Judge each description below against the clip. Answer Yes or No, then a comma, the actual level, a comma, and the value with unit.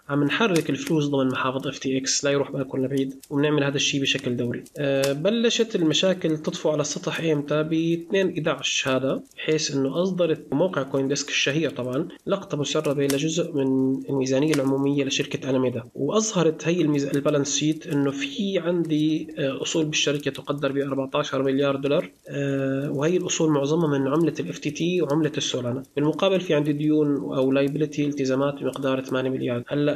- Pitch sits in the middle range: Yes, medium, 145 Hz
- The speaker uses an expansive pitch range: No, narrow, 2.5 semitones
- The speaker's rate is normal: No, fast, 160 wpm